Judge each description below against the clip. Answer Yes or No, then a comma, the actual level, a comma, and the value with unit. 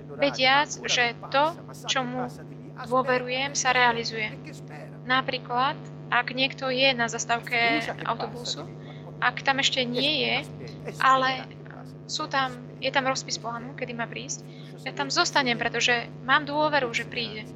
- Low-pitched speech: No, very high, 260 Hz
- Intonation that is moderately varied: No, narrow, 2.1 semitones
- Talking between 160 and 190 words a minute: No, average, 130 wpm